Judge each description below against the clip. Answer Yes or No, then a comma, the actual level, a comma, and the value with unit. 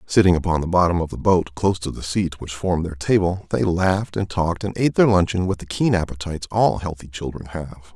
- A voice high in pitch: No, very low, 90 Hz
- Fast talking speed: Yes, fast, 235 wpm